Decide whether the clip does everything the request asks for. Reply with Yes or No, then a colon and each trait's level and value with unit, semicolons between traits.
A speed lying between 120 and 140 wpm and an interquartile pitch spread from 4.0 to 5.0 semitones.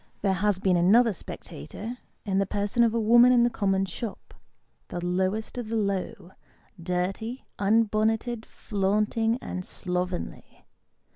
No: slow, 135 wpm; average, 3.3 semitones